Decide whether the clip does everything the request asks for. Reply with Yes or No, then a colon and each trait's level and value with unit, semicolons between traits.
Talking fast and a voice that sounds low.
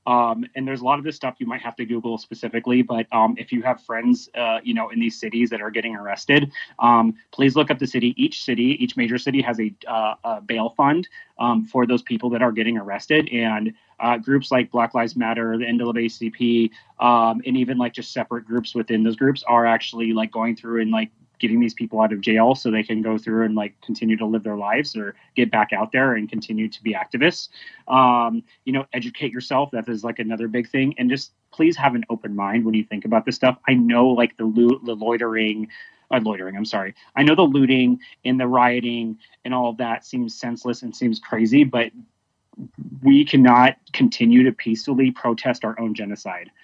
Yes: fast, 220 wpm; low, 120 Hz